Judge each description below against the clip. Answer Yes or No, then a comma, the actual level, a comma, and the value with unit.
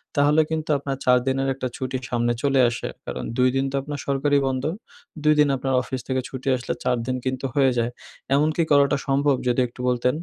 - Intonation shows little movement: Yes, narrow, 2.0 semitones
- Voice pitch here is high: No, low, 135 Hz